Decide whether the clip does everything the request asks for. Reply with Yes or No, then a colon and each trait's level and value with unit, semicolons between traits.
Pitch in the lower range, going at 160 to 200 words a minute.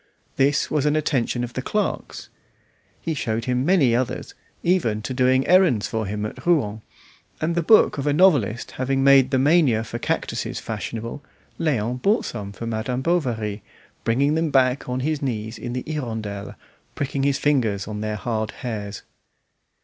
Yes: low, 130 Hz; average, 165 wpm